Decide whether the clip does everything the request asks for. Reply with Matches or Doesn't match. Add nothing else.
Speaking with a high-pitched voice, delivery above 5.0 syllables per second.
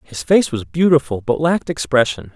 Doesn't match